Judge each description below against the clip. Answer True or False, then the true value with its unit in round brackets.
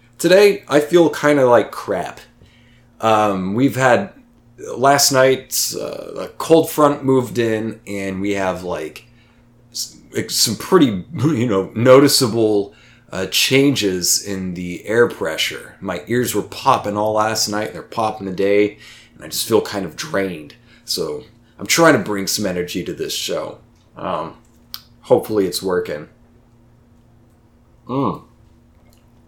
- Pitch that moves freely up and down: False (4.1 semitones)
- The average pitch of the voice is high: False (120 Hz)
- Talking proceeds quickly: False (135 wpm)